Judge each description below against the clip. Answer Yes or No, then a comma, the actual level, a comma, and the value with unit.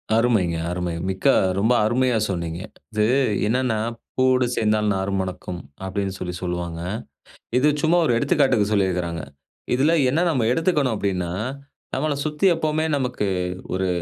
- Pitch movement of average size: No, wide, 5.9 semitones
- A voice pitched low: Yes, low, 105 Hz